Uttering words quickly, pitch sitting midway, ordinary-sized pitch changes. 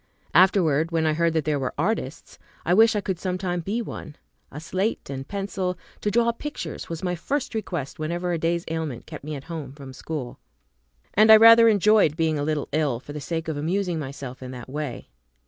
Yes: fast, 210 wpm; medium, 165 Hz; average, 4.8 semitones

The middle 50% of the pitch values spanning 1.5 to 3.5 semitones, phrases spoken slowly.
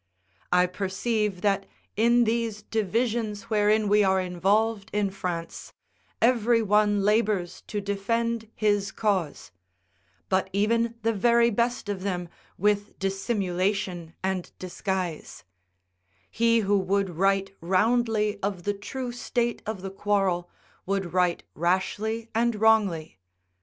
Yes: average, 2.8 semitones; slow, 120 wpm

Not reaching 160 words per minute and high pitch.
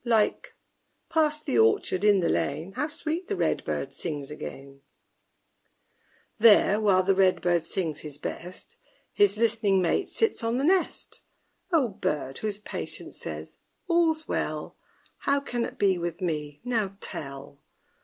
Yes: average, 145 wpm; high, 200 Hz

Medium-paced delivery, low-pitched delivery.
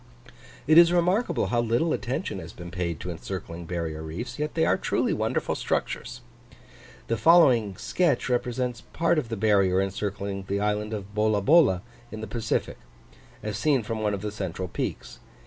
Yes: average, 165 wpm; low, 110 Hz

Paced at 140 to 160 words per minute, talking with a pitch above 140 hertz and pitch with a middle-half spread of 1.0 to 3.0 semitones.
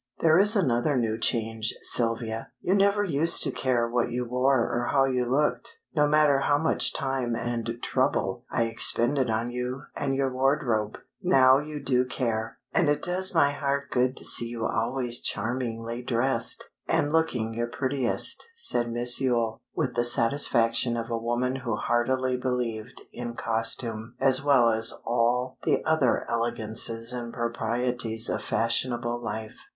No: average, 155 wpm; low, 120 Hz; narrow, 2.6 semitones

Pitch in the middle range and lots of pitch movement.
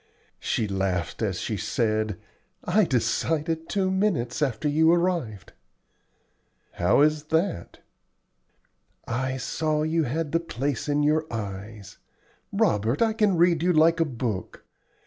Yes: medium, 150 Hz; wide, 6.7 semitones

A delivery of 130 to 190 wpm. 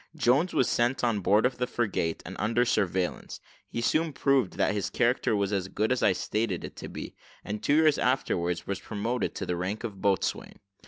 No: fast, 205 wpm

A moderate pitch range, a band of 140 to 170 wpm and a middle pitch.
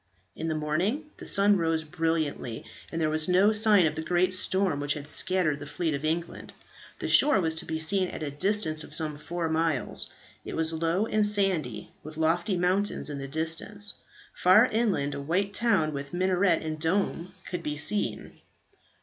No: average, 3.8 semitones; average, 185 wpm; medium, 165 Hz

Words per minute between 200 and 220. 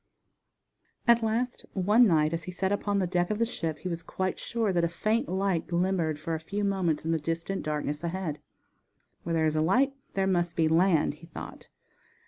Yes: fast, 205 wpm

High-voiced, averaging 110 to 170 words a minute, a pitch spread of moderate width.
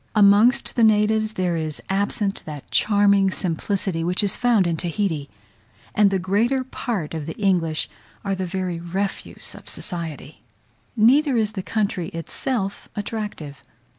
Yes: high, 195 Hz; average, 140 wpm; average, 3.9 semitones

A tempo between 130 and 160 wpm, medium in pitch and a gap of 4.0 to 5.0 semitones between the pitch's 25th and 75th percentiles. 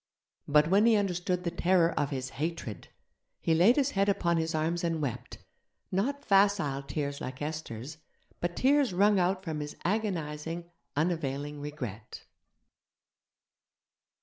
Yes: slow, 135 wpm; medium, 165 Hz; average, 4.6 semitones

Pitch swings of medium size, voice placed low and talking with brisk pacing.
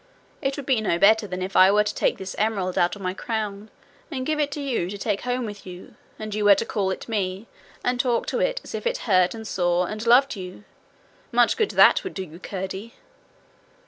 No: average, 4.5 semitones; high, 210 Hz; fast, 235 wpm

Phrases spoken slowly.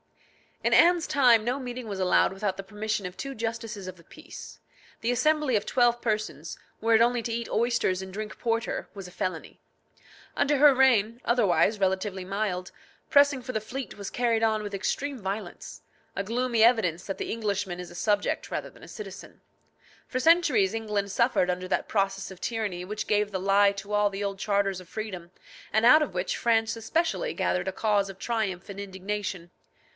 No: average, 190 wpm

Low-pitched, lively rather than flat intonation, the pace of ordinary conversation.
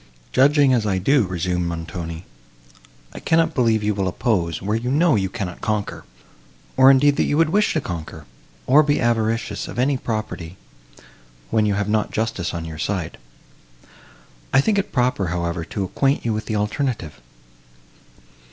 Yes: low, 110 Hz; wide, 6.6 semitones; average, 165 wpm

